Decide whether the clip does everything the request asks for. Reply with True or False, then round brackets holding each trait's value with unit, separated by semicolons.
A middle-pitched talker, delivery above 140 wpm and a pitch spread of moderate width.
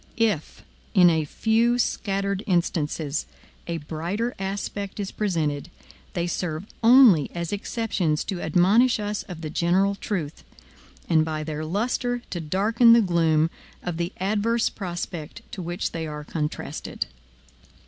False (180 Hz; 135 wpm; 4.6 semitones)